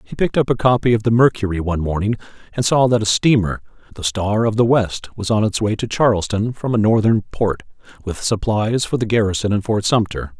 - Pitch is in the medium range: No, low, 110 Hz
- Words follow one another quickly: Yes, fast, 220 wpm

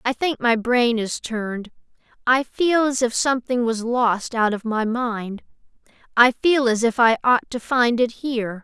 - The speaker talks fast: No, average, 190 wpm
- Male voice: No, female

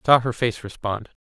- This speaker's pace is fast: Yes, fast, 245 wpm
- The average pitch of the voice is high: No, low, 115 Hz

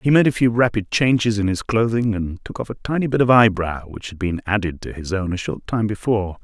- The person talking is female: No, male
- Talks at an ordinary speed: No, fast, 260 wpm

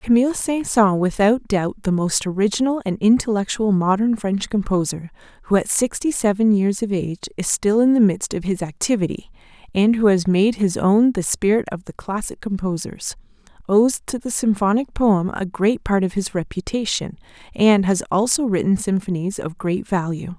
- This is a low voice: No, high, 205 Hz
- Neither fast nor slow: Yes, average, 175 wpm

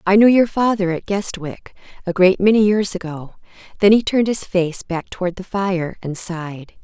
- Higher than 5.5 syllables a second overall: No, 5.0 syllables/s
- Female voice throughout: Yes, female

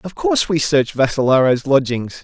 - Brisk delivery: No, average, 160 wpm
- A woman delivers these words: No, male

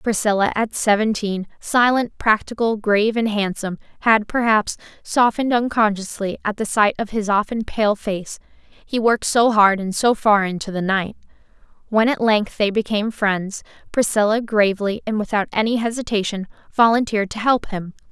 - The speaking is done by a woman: Yes, female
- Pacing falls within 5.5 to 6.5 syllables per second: No, 5.1 syllables/s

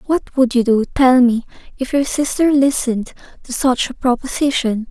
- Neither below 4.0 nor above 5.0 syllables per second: Yes, 4.8 syllables/s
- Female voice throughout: Yes, female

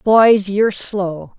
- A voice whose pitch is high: Yes, high, 200 Hz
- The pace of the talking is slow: Yes, slow, 130 wpm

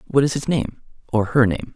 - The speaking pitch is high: No, low, 130 Hz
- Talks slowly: No, fast, 205 wpm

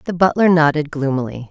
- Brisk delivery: No, average, 160 wpm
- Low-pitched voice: No, medium, 155 Hz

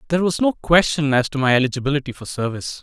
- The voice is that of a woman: No, male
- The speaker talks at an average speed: No, fast, 210 wpm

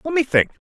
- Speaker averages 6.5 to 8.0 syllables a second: Yes, 7.3 syllables/s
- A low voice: No, high, 230 Hz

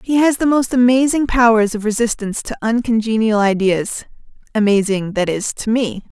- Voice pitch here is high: Yes, high, 225 Hz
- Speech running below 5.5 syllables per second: Yes, 5.2 syllables/s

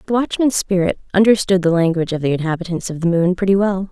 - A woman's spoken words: Yes, female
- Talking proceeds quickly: Yes, fast, 215 wpm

